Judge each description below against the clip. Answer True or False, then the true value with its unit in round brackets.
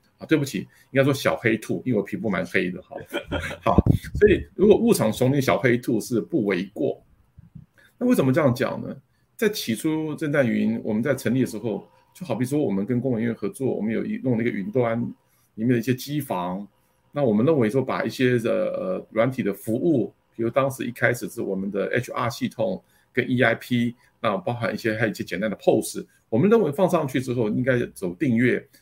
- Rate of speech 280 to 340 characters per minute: True (310 characters per minute)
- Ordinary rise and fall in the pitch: True (4.5 semitones)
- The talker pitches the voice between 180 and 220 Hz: False (125 Hz)